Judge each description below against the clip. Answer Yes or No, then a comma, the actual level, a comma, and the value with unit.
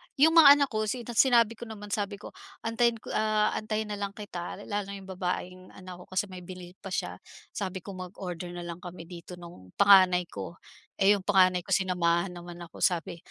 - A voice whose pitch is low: No, high, 190 Hz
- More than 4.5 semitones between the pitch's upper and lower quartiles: No, average, 2.9 semitones